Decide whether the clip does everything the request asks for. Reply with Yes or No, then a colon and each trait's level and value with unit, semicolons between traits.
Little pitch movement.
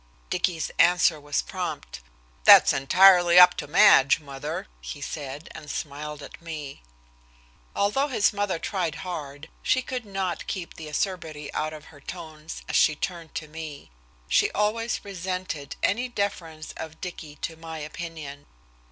No: average, 3.8 semitones